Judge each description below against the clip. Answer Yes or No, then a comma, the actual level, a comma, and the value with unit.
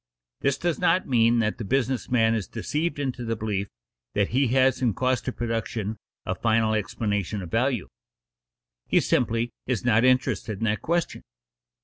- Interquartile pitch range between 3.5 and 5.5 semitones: No, average, 3.1 semitones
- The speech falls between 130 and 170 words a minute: Yes, average, 165 wpm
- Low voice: Yes, low, 115 Hz